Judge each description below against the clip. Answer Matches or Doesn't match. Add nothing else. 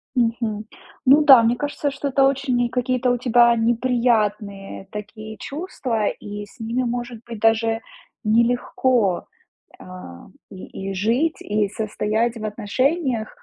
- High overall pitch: Matches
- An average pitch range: Matches